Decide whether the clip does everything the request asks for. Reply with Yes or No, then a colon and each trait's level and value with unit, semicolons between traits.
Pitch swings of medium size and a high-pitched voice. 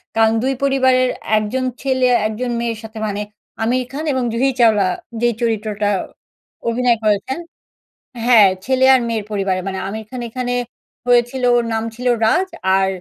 Yes: average, 3.0 semitones; high, 235 Hz